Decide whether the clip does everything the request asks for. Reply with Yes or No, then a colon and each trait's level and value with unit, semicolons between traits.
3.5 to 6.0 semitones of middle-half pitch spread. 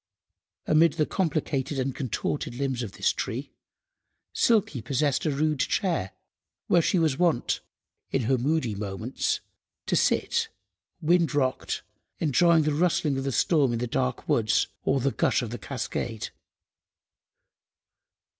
Yes: average, 4.5 semitones